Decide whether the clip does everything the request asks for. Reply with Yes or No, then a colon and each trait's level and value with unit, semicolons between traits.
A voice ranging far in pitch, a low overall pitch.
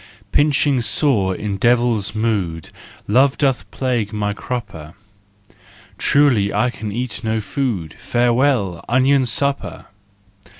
No: average, 4.4 semitones; low, 115 Hz